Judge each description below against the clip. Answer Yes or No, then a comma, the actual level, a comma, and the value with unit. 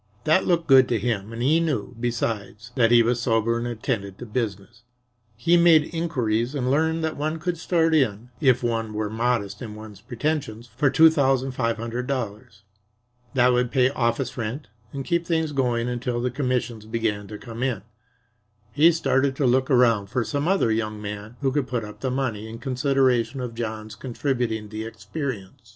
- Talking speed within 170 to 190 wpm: Yes, average, 185 wpm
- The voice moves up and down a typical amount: Yes, average, 3.5 semitones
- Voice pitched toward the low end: Yes, low, 125 Hz